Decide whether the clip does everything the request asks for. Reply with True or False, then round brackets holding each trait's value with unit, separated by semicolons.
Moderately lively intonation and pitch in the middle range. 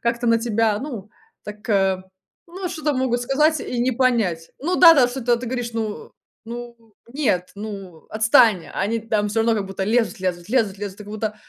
False (3.2 semitones; 225 Hz)